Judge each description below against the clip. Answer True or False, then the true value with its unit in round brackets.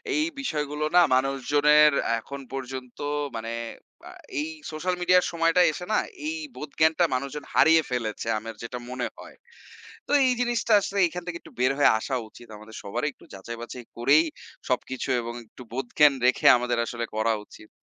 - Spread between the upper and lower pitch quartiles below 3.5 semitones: False (4.7 semitones)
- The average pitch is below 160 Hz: True (140 Hz)